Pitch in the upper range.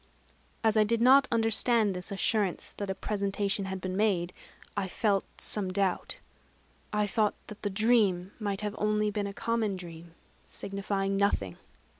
Yes: high, 200 Hz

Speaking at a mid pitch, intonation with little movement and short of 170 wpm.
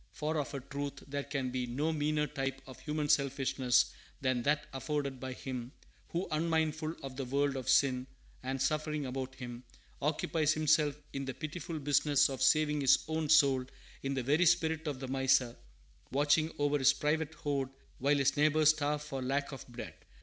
No: medium, 145 Hz; narrow, 2.3 semitones; average, 180 wpm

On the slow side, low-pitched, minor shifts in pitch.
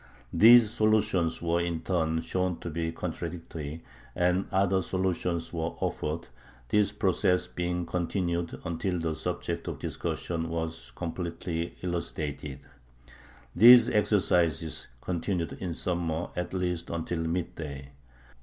Yes: slow, 115 wpm; very low, 85 Hz; narrow, 2.0 semitones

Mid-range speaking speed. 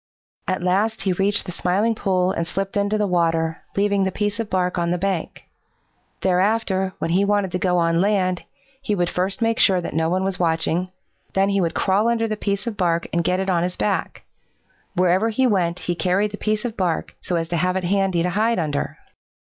No: fast, 220 wpm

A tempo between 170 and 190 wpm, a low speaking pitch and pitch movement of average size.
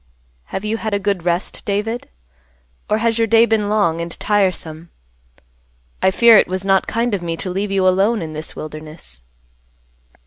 No: average, 175 wpm; high, 195 Hz; average, 4.0 semitones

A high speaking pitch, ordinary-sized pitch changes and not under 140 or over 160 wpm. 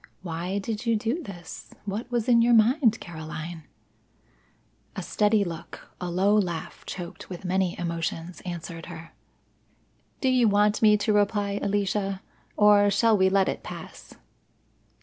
Yes: high, 200 Hz; average, 3.6 semitones; average, 145 wpm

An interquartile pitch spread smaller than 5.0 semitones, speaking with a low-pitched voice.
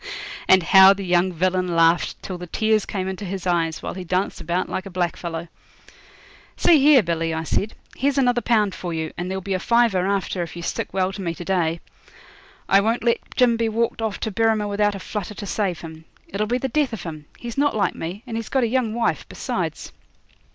No: average, 4.2 semitones; high, 195 Hz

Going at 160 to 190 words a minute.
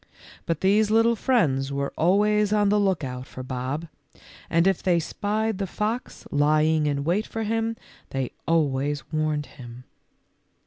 No: average, 145 wpm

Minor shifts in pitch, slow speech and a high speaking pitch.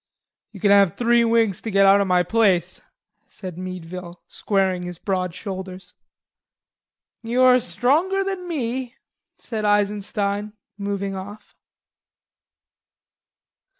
No: average, 3.7 semitones; slow, 115 wpm; high, 200 Hz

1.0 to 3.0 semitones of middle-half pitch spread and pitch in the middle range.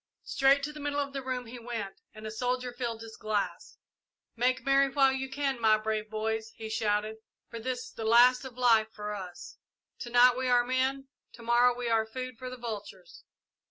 No: average, 2.7 semitones; high, 245 Hz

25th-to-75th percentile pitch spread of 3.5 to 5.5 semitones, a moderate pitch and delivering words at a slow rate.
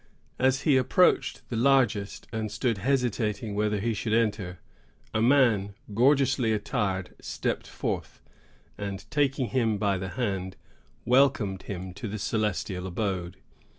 No: average, 4.4 semitones; low, 110 Hz; slow, 130 wpm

